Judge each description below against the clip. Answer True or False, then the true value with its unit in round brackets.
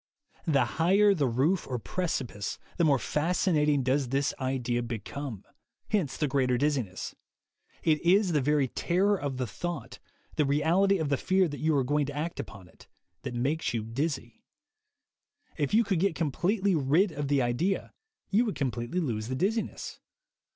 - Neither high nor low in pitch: True (145 Hz)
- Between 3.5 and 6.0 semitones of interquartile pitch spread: True (5.2 semitones)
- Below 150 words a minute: False (175 wpm)